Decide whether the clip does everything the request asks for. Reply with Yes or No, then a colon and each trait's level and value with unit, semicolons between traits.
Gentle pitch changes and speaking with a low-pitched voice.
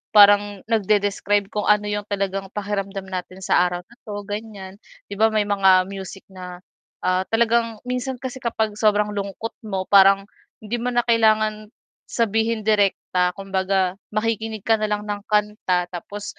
No: narrow, 2.0 semitones; high, 205 Hz